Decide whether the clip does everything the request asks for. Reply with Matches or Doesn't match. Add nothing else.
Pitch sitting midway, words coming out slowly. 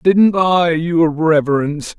Matches